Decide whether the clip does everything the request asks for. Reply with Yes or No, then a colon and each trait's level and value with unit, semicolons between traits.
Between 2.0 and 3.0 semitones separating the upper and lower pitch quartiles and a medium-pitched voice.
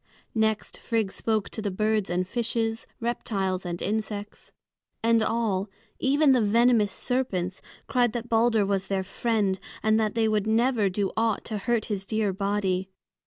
No: average, 2.7 semitones; high, 215 Hz